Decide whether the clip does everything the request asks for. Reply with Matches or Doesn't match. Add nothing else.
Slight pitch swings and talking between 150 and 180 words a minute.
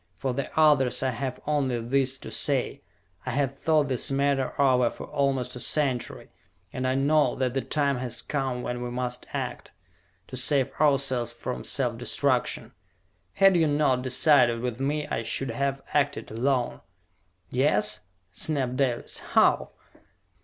Matches